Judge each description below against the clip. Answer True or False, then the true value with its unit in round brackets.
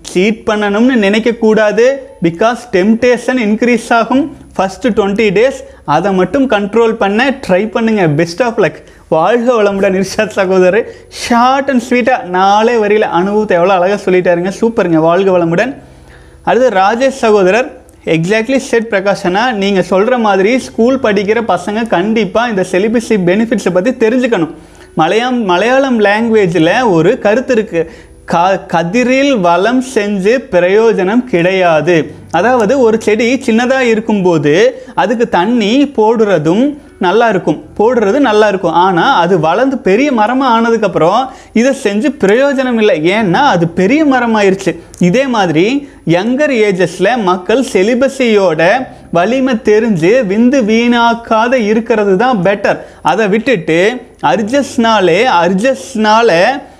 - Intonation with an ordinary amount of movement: True (4.6 semitones)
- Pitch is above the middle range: True (220 Hz)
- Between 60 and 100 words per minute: False (115 wpm)